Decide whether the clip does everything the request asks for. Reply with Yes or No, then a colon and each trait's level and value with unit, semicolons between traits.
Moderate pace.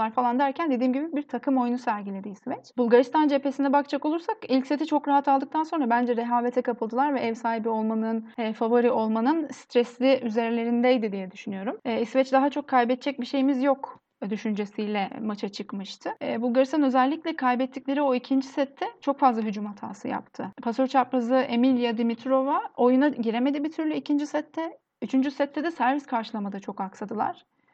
No: fast, 160 wpm